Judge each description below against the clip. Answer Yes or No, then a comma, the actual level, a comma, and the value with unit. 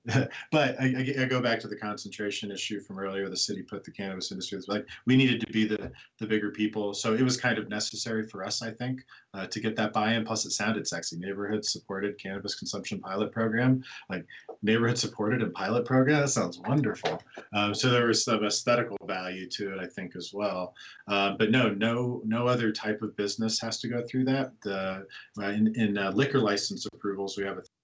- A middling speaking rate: No, fast, 220 wpm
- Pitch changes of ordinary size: Yes, average, 3.0 semitones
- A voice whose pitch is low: Yes, low, 110 Hz